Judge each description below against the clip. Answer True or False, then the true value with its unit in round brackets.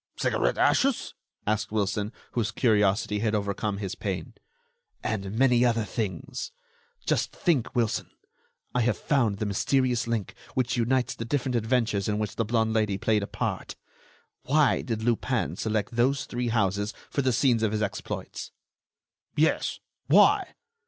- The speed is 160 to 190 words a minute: False (145 wpm)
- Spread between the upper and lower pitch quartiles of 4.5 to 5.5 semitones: False (3.0 semitones)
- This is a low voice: True (110 Hz)